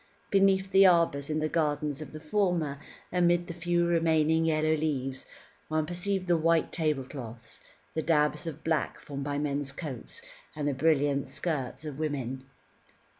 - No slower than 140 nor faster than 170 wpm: Yes, average, 155 wpm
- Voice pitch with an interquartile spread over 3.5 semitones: No, average, 2.9 semitones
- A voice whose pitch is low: No, medium, 155 Hz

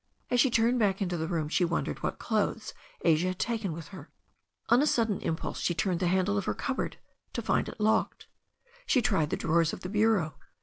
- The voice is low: No, high, 190 Hz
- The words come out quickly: Yes, fast, 215 wpm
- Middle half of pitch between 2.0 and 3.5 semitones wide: No, average, 4.8 semitones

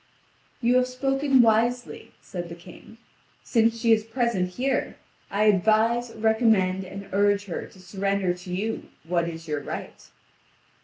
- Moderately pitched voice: No, high, 215 Hz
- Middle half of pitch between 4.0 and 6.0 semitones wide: Yes, average, 4.3 semitones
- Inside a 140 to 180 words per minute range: Yes, average, 145 wpm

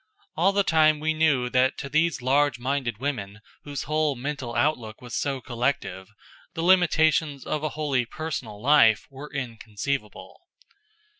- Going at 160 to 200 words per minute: No, average, 145 wpm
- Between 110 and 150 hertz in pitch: Yes, medium, 140 Hz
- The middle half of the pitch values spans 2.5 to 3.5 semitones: No, average, 4.1 semitones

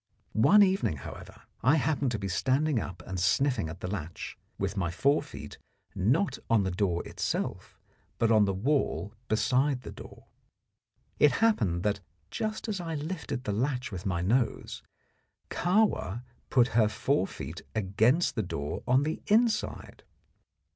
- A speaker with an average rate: Yes, average, 155 wpm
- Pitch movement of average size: No, wide, 7.4 semitones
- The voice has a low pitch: Yes, low, 120 Hz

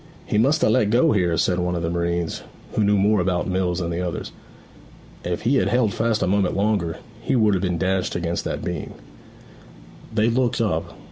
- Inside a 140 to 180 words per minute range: No, fast, 205 wpm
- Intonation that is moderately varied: Yes, average, 3.8 semitones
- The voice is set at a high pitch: No, very low, 95 Hz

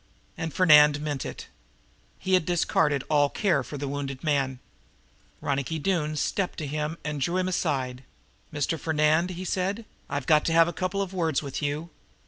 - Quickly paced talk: No, average, 175 wpm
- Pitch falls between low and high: Yes, medium, 155 Hz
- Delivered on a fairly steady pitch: No, average, 3.4 semitones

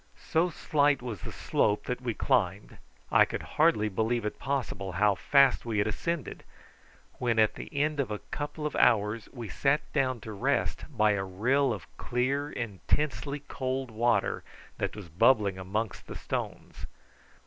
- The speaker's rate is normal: Yes, average, 160 wpm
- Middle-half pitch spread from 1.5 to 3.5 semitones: No, average, 5.0 semitones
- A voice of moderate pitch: No, low, 120 Hz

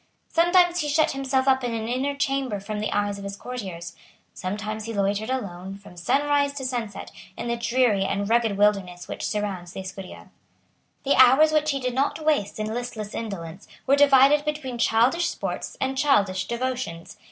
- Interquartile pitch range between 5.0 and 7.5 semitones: Yes, average, 5.3 semitones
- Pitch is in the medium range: No, high, 235 Hz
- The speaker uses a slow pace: No, average, 175 wpm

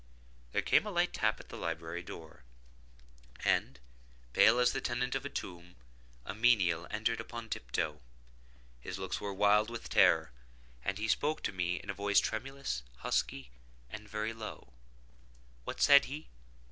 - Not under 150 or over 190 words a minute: Yes, average, 155 wpm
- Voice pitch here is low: Yes, low, 100 Hz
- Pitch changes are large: Yes, wide, 6.5 semitones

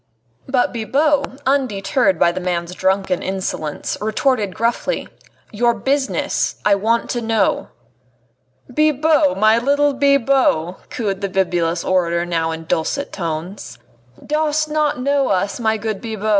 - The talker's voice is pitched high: Yes, high, 220 Hz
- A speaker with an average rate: No, slow, 130 wpm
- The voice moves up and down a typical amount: No, wide, 6.7 semitones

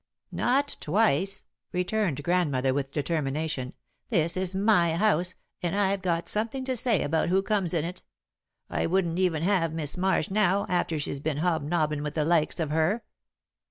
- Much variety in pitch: No, average, 3.9 semitones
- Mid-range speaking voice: Yes, medium, 175 Hz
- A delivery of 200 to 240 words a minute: No, average, 160 wpm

